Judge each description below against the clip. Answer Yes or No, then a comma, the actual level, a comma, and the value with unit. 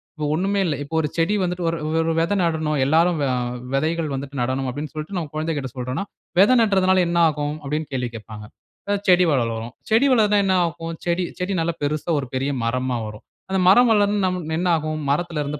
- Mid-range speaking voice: Yes, medium, 160 Hz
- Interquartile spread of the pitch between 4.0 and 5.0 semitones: Yes, average, 4.4 semitones